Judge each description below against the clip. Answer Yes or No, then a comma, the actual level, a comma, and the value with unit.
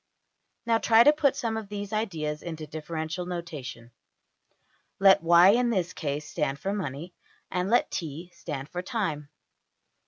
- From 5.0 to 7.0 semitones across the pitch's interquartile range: Yes, wide, 5.4 semitones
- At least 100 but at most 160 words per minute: Yes, average, 150 wpm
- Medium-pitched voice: Yes, medium, 175 Hz